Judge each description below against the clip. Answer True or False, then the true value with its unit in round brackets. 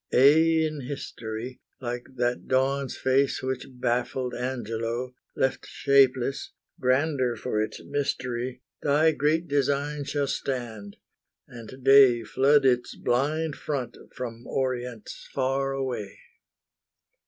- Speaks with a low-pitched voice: True (130 Hz)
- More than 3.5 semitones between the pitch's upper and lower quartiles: False (2.4 semitones)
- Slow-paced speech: True (110 wpm)